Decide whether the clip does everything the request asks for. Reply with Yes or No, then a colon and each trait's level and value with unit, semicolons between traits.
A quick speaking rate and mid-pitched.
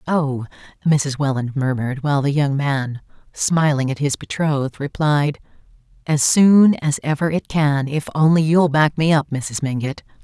No: average, 160 wpm; medium, 145 Hz